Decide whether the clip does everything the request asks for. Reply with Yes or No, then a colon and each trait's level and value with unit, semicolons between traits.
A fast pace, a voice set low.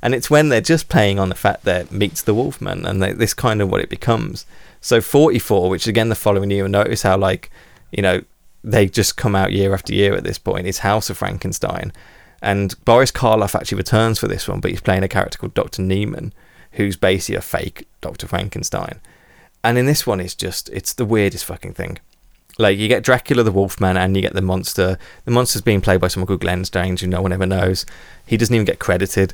Yes: fast, 225 wpm; low, 100 Hz